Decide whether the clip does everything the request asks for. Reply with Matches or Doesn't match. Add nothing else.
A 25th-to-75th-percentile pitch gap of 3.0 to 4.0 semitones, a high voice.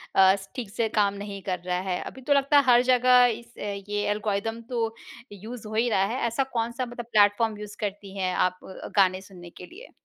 Matches